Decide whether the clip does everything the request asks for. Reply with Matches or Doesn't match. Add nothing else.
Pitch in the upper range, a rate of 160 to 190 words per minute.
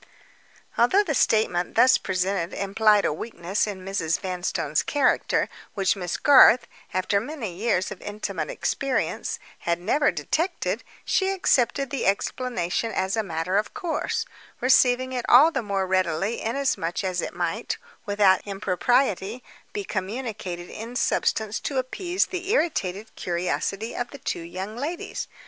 Doesn't match